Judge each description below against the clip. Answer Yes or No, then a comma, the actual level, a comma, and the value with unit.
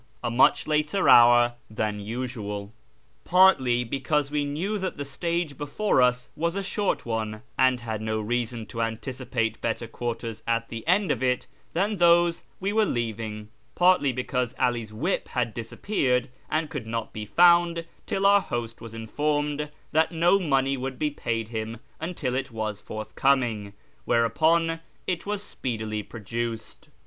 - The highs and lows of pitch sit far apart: Yes, wide, 6.2 semitones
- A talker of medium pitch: No, low, 125 Hz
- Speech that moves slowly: No, average, 155 wpm